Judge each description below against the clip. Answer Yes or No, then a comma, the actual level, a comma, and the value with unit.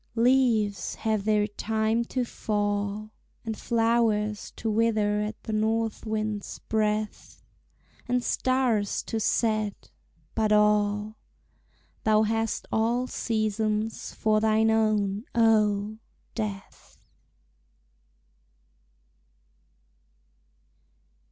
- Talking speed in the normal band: No, slow, 85 wpm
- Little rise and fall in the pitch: Yes, narrow, 1.1 semitones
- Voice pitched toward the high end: Yes, high, 215 Hz